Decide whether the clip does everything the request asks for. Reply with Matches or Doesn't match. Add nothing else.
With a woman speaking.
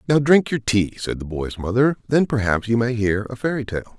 Doesn't match